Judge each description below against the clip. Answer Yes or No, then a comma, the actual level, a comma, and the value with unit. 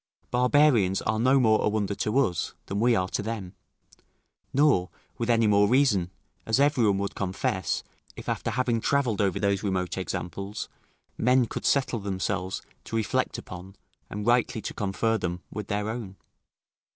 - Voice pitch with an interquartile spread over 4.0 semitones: No, average, 3.6 semitones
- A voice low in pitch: Yes, low, 105 Hz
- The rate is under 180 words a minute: Yes, average, 165 wpm